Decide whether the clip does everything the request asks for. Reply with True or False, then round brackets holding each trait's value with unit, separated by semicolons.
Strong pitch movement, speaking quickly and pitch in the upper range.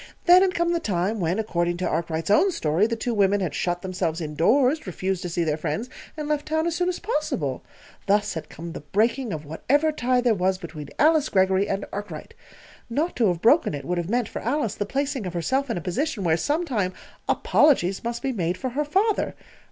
True (8.2 semitones; 215 wpm; 205 Hz)